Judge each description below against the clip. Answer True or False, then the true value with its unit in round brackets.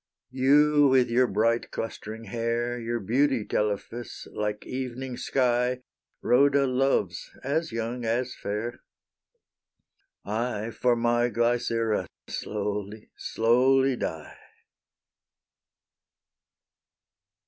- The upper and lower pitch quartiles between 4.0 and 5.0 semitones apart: False (2.4 semitones)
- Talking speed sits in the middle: False (85 wpm)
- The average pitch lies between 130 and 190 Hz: False (120 Hz)